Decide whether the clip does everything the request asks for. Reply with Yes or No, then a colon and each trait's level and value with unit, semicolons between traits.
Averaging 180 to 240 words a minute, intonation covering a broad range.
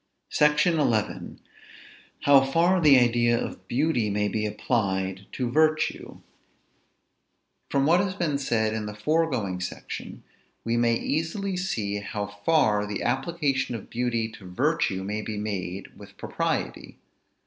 No: slow, 135 wpm; wide, 6.6 semitones